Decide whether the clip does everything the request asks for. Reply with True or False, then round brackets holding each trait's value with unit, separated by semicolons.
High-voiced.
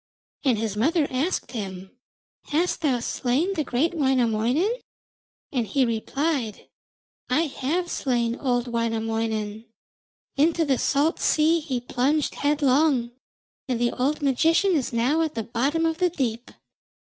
True (265 Hz)